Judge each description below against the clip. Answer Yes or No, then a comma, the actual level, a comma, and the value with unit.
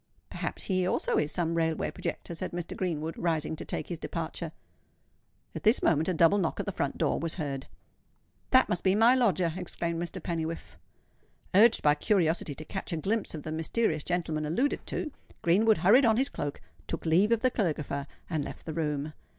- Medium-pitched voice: Yes, medium, 170 Hz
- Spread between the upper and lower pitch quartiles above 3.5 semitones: Yes, average, 4.1 semitones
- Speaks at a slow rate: No, average, 190 wpm